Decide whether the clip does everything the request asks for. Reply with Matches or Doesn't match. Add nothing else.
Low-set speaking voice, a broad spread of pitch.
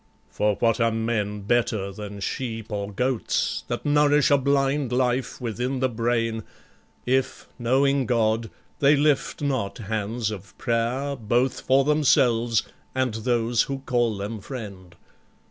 Doesn't match